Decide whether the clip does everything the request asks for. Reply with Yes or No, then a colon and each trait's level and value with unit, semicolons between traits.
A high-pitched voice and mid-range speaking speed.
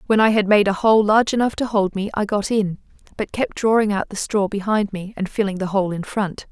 No: high, 205 Hz; fast, 260 wpm